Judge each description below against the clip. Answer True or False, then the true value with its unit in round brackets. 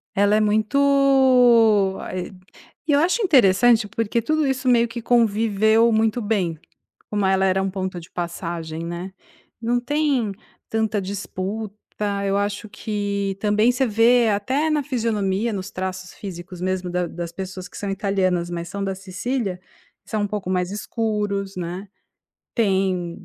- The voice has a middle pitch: False (205 Hz)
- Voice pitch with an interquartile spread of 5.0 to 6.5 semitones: False (3.7 semitones)